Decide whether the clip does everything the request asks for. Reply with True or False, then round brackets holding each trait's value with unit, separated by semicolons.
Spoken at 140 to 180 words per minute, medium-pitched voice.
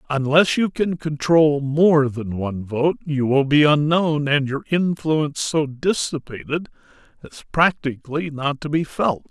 True (150 wpm; 150 Hz)